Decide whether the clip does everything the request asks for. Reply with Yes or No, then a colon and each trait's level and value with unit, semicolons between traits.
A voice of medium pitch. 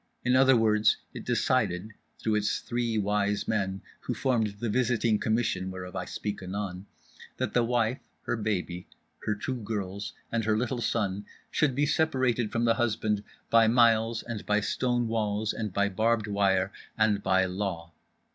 No: low, 110 Hz